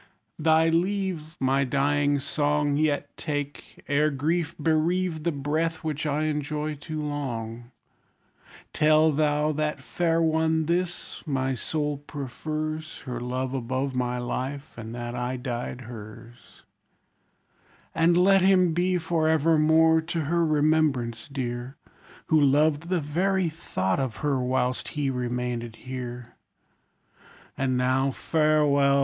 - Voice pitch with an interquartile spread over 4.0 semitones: No, average, 3.6 semitones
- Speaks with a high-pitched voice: No, medium, 145 Hz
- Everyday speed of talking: No, slow, 125 wpm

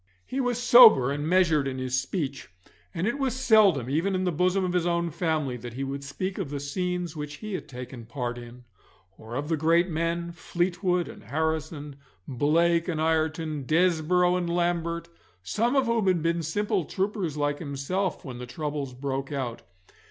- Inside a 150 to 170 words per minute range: No, average, 180 wpm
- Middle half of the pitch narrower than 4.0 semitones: No, average, 4.4 semitones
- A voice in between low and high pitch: Yes, medium, 160 Hz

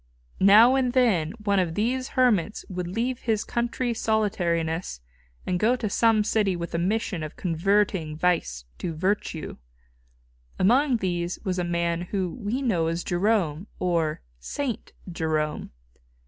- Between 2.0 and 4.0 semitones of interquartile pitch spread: No, average, 4.8 semitones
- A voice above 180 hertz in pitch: Yes, high, 190 Hz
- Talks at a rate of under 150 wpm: Yes, average, 140 wpm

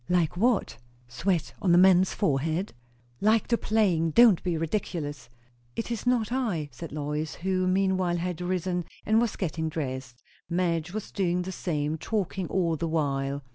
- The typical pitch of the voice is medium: Yes, medium, 175 Hz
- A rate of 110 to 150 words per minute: No, average, 160 wpm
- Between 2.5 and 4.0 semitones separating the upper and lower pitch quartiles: Yes, average, 3.5 semitones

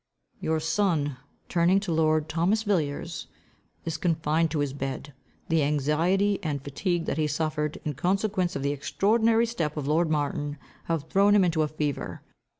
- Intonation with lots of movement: No, average, 3.7 semitones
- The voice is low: No, medium, 160 Hz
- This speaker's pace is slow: No, average, 160 wpm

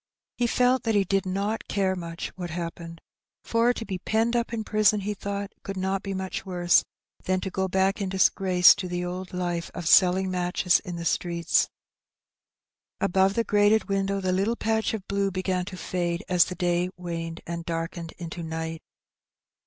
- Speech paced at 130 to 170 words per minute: No, average, 185 wpm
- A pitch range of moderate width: No, narrow, 2.3 semitones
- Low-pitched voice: No, medium, 185 Hz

